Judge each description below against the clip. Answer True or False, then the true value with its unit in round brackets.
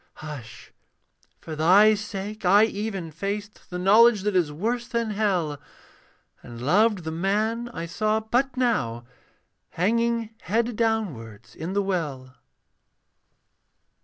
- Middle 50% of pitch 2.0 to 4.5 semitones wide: False (5.5 semitones)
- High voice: True (200 Hz)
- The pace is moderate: False (120 wpm)